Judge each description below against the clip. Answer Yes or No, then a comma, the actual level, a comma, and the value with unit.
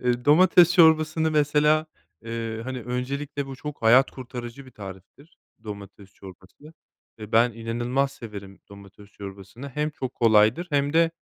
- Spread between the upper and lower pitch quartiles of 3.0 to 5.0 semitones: No, wide, 5.4 semitones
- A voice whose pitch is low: Yes, low, 125 Hz